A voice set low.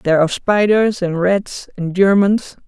No: high, 190 Hz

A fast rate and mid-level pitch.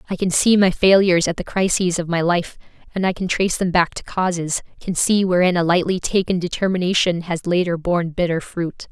Yes: fast, 210 wpm; medium, 180 Hz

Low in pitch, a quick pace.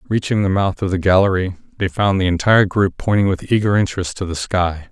Yes: very low, 95 Hz; fast, 220 wpm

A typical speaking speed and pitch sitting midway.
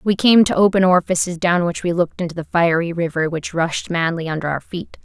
No: fast, 225 wpm; medium, 170 Hz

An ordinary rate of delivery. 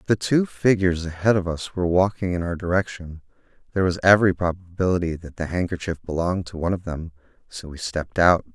Yes: average, 190 wpm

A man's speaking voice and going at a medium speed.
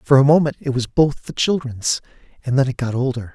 No: male; fast, 235 wpm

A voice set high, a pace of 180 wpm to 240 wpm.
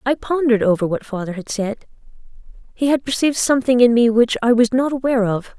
Yes: high, 240 Hz; fast, 205 wpm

